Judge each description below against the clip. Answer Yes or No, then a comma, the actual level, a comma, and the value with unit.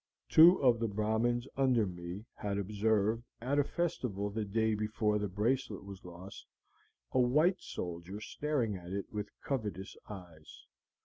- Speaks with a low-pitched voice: Yes, low, 105 Hz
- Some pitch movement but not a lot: Yes, average, 3.5 semitones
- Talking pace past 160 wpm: No, average, 145 wpm